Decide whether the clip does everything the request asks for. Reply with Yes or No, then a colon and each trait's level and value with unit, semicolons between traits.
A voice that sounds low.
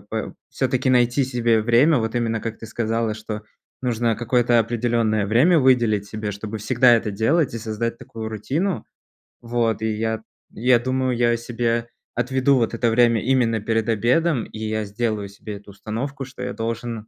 Yes: low, 115 Hz